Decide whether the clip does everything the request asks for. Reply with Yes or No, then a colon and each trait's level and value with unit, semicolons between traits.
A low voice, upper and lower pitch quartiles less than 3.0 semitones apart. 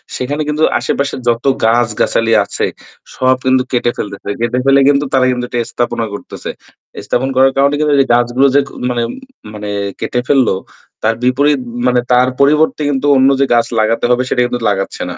Yes: low, 125 Hz; narrow, 2.5 semitones